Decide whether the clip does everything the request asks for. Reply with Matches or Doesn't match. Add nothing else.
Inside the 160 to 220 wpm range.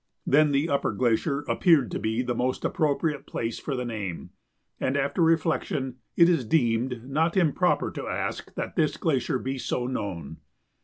Matches